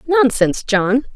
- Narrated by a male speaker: No, female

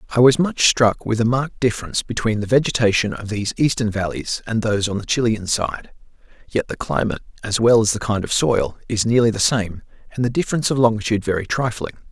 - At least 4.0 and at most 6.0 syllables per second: No, 6.3 syllables/s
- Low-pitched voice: Yes, low, 115 Hz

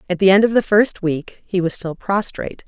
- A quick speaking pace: Yes, fast, 245 wpm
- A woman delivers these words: Yes, female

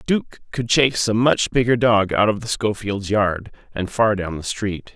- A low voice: Yes, low, 110 Hz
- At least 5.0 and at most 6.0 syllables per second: No, 4.5 syllables/s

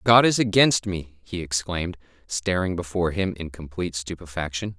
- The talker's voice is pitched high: No, very low, 90 Hz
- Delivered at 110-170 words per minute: Yes, average, 150 wpm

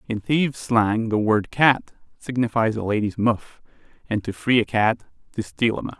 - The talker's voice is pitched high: No, low, 115 Hz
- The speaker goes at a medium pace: Yes, average, 190 wpm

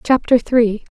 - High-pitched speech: Yes, high, 235 Hz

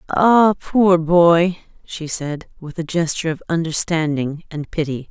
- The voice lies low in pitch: No, medium, 165 Hz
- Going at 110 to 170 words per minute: Yes, average, 140 wpm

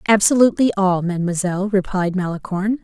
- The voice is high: Yes, high, 195 Hz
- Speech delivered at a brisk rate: No, slow, 105 wpm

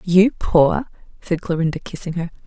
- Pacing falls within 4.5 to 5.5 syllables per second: Yes, 4.6 syllables/s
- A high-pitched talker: No, medium, 175 Hz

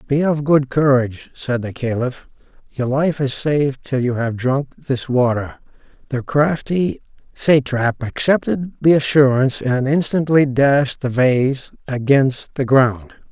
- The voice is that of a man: Yes, male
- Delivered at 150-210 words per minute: No, average, 140 wpm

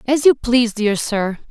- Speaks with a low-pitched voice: No, high, 235 Hz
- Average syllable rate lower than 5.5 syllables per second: Yes, 4.5 syllables/s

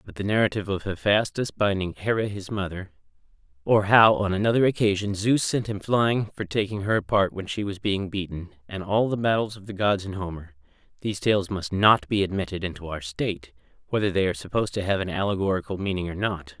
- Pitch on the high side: No, low, 100 Hz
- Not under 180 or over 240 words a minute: Yes, average, 200 wpm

